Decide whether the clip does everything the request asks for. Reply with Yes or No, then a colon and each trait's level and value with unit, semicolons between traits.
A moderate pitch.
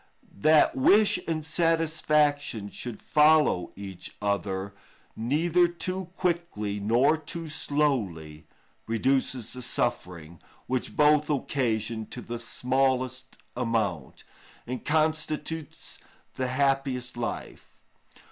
No: low, 130 Hz